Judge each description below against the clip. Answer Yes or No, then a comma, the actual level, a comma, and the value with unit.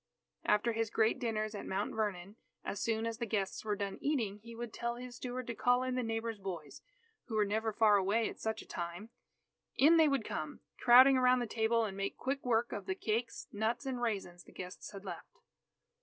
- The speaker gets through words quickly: Yes, fast, 215 wpm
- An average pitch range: Yes, average, 3.0 semitones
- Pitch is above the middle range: Yes, high, 225 Hz